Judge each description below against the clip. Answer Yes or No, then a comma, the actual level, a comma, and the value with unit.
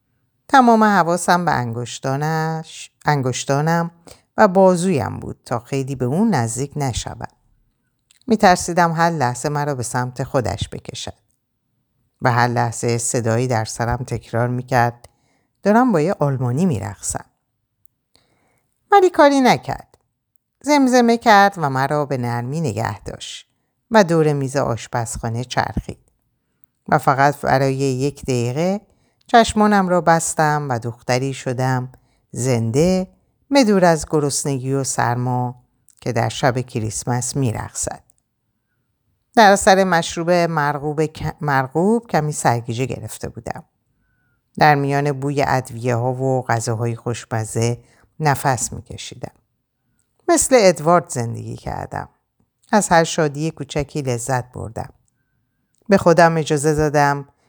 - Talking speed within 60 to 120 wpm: Yes, average, 110 wpm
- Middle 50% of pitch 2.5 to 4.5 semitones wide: No, average, 5.1 semitones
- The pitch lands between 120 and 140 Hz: Yes, low, 135 Hz